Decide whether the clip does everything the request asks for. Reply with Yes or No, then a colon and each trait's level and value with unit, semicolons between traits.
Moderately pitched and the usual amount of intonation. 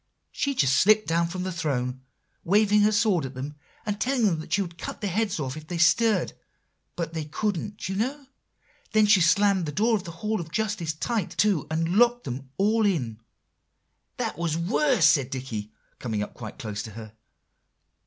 No: medium, 170 Hz; wide, 6.1 semitones